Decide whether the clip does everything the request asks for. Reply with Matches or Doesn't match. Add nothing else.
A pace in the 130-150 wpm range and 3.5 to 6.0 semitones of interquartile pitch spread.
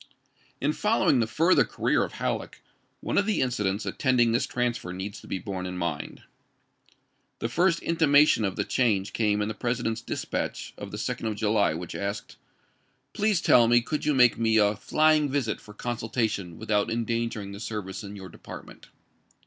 Doesn't match